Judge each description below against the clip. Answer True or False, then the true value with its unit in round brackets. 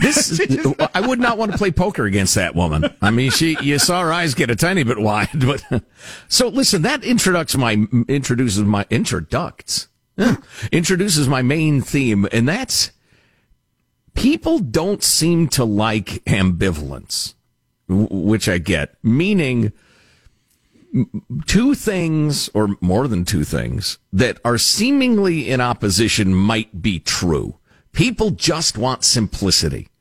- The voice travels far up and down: True (8.2 semitones)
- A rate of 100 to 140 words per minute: True (135 wpm)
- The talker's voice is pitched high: False (125 Hz)